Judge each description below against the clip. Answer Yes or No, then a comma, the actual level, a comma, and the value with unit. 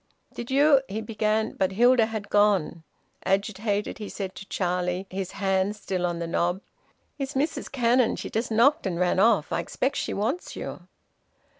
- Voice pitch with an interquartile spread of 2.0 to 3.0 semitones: No, average, 3.7 semitones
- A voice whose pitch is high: Yes, high, 205 Hz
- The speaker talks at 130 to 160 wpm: No, average, 175 wpm